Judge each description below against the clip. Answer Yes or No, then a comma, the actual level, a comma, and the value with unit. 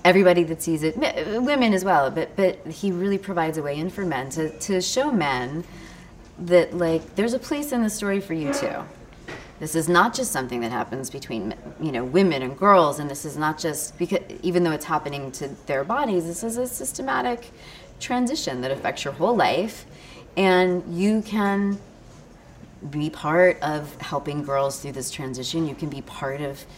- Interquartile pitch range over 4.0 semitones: Yes, average, 5.1 semitones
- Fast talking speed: No, average, 190 wpm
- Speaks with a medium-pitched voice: Yes, medium, 165 Hz